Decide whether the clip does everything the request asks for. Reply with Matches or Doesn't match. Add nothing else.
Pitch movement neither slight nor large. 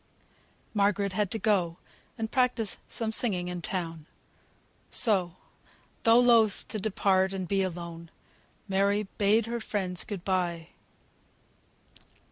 Matches